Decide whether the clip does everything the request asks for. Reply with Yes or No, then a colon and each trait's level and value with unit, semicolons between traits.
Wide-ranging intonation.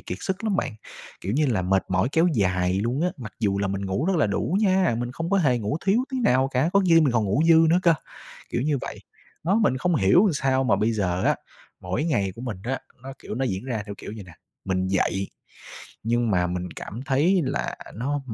Yes: wide, 8.1 semitones